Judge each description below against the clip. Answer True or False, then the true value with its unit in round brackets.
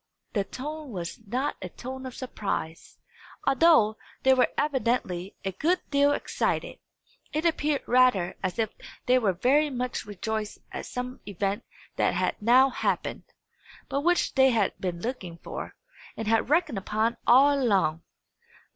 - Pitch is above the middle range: True (245 Hz)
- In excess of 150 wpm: False (145 wpm)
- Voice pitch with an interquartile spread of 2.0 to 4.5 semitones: False (5.3 semitones)